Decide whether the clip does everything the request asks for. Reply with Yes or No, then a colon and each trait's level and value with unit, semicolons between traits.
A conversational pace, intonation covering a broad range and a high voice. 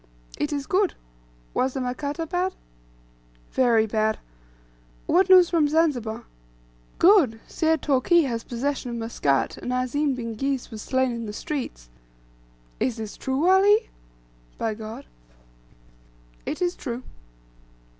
No: slow, 125 wpm; wide, 5.9 semitones; very high, 265 Hz